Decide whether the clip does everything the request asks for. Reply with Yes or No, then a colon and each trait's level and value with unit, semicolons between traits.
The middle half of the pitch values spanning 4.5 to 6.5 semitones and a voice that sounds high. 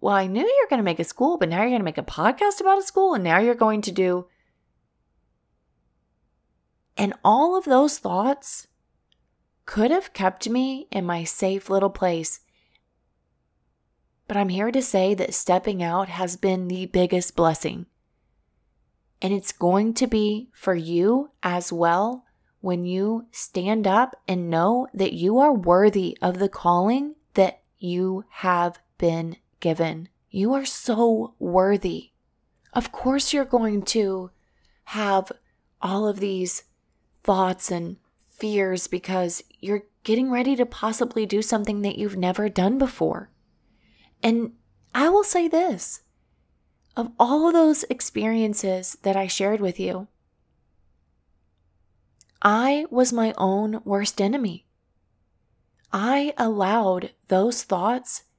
Yes: average, 4.8 semitones; high, 195 Hz